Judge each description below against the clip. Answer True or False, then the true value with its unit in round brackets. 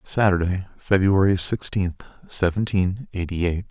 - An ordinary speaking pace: False (95 wpm)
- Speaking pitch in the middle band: False (95 Hz)